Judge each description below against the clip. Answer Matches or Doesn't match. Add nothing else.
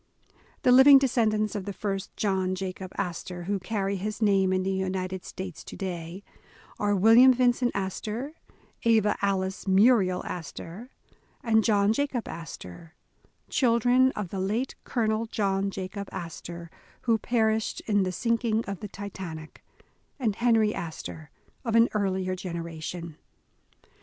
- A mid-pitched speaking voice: Doesn't match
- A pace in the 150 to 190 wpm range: Doesn't match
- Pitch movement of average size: Matches